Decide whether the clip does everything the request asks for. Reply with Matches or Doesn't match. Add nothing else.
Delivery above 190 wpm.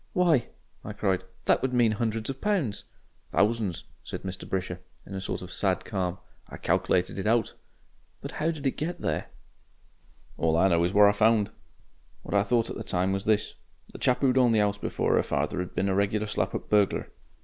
Matches